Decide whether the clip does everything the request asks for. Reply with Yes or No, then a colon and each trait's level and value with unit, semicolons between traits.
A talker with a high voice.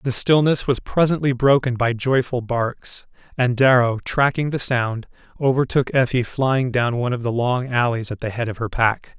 No: low, 125 Hz